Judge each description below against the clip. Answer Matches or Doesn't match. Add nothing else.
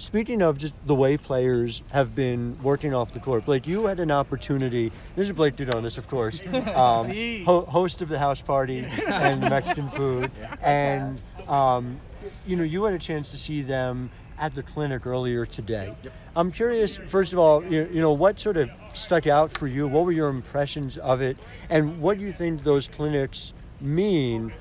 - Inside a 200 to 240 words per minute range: Doesn't match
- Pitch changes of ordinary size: Matches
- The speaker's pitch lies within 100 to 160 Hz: Matches